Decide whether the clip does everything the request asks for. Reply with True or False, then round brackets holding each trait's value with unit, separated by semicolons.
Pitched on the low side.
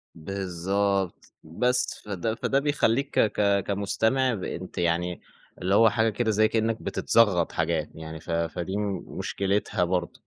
True (100 Hz)